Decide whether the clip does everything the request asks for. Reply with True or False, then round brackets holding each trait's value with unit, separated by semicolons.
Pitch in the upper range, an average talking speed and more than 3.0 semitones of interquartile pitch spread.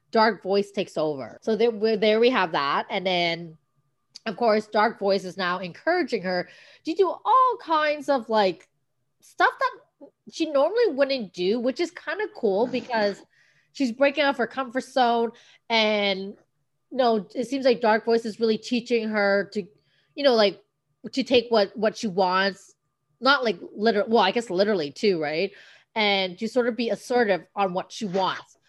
True (220 Hz; 180 wpm; 4.8 semitones)